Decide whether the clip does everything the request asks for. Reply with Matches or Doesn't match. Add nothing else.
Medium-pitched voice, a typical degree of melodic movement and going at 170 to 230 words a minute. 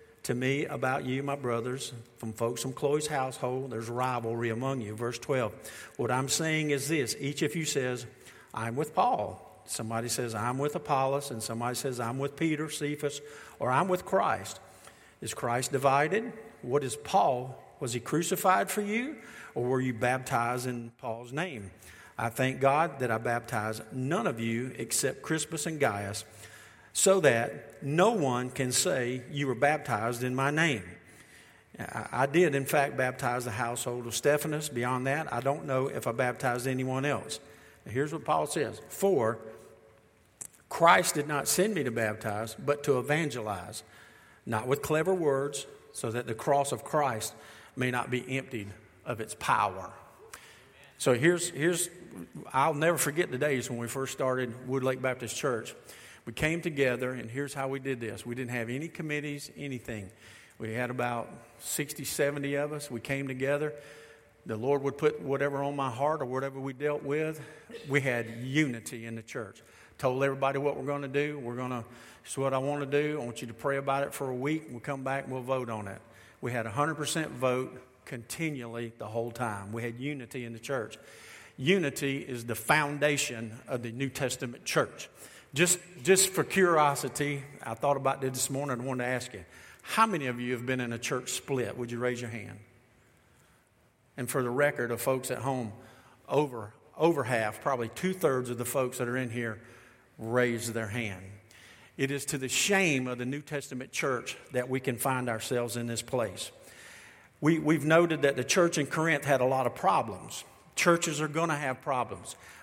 Doesn't match